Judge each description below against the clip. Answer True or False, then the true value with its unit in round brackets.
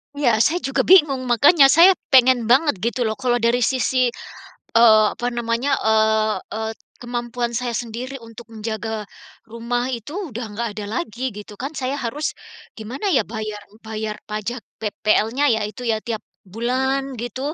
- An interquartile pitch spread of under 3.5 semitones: True (3.0 semitones)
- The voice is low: False (235 Hz)